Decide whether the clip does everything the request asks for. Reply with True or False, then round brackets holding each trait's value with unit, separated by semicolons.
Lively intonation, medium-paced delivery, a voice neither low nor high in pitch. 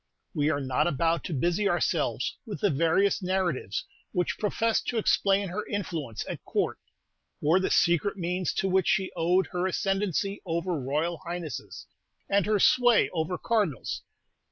False (3.3 semitones; 155 wpm; 180 Hz)